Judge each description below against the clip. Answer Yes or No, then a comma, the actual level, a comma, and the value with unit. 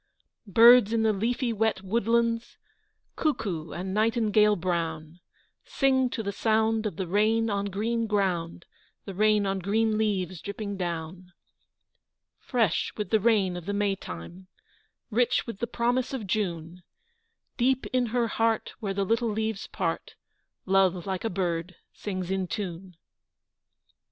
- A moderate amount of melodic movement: Yes, average, 3.5 semitones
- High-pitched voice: Yes, high, 205 Hz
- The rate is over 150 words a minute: No, average, 145 wpm